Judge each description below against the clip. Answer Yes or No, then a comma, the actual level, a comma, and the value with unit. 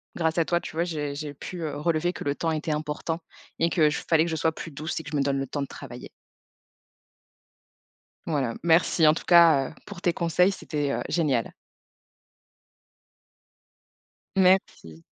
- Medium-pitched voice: Yes, medium, 160 Hz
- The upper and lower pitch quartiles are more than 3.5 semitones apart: No, average, 2.8 semitones